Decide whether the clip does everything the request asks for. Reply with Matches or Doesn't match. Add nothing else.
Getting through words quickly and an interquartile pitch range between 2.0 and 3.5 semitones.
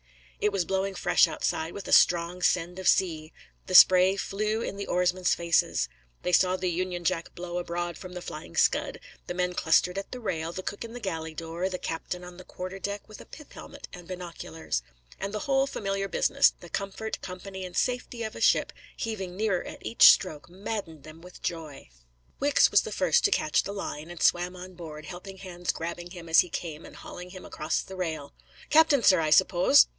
Matches